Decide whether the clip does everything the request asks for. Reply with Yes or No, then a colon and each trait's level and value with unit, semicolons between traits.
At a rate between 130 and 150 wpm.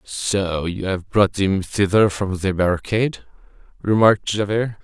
Yes: slow, 135 wpm